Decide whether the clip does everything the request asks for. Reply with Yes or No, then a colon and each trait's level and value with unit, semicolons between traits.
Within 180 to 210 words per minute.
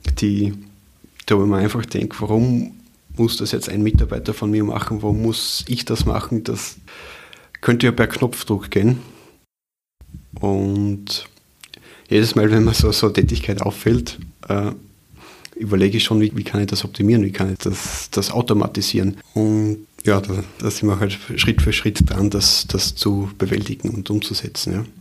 No: average, 170 wpm